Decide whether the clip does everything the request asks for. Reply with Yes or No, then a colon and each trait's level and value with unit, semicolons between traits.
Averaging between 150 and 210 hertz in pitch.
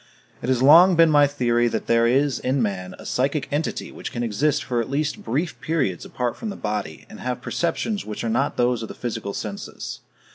No: low, 125 Hz